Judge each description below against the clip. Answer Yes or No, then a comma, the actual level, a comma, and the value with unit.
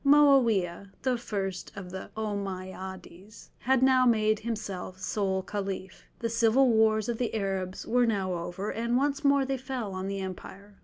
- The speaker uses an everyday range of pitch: Yes, average, 4.1 semitones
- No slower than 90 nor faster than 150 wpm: No, average, 160 wpm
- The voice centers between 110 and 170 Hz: No, high, 210 Hz